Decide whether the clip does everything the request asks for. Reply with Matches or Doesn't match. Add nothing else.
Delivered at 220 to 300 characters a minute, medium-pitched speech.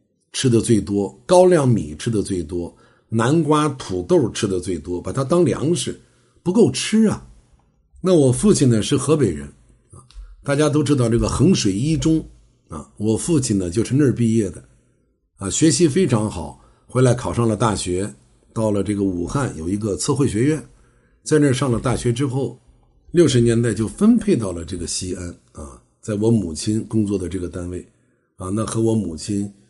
Doesn't match